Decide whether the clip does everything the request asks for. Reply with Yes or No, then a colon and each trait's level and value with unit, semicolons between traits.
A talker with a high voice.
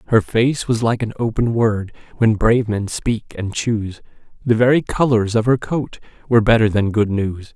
No: low, 110 Hz